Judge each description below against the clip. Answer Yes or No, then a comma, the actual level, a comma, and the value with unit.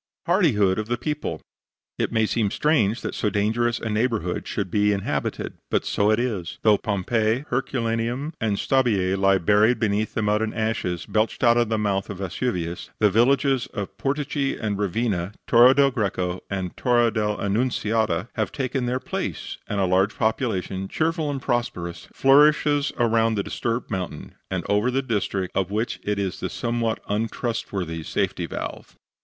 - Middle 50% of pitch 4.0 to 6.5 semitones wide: No, average, 3.6 semitones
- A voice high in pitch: No, low, 110 Hz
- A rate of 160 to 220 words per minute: Yes, average, 165 wpm